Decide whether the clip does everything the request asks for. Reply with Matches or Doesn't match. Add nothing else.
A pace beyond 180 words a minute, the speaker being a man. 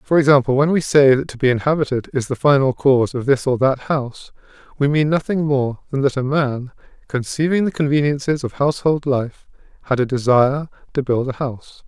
Matches